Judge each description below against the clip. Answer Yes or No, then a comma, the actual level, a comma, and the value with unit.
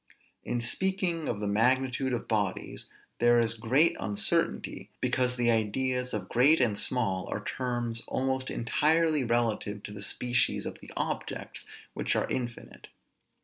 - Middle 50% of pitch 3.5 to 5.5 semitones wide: No, average, 2.8 semitones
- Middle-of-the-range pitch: No, low, 120 Hz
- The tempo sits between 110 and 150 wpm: Yes, average, 145 wpm